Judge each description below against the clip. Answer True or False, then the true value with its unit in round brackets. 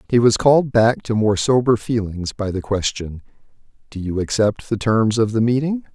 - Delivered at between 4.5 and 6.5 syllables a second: True (5.0 syllables/s)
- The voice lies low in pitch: True (115 Hz)